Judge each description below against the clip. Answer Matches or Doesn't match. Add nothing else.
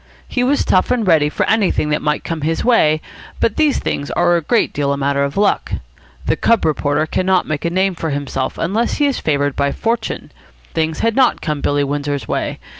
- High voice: Doesn't match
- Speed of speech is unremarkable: Doesn't match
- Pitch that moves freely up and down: Matches